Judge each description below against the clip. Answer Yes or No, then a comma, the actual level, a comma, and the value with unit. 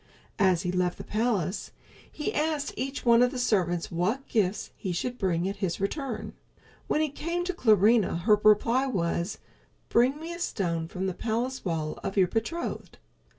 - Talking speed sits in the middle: Yes, average, 175 wpm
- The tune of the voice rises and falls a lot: Yes, wide, 6.1 semitones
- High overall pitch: Yes, high, 215 Hz